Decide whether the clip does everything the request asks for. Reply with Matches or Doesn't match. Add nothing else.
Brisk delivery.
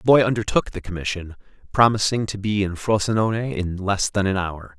Doesn't match